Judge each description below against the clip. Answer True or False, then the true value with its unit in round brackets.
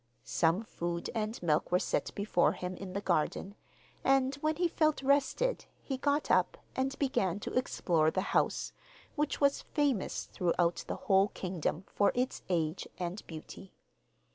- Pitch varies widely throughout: True (7.6 semitones)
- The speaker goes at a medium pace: True (155 wpm)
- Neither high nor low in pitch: False (200 Hz)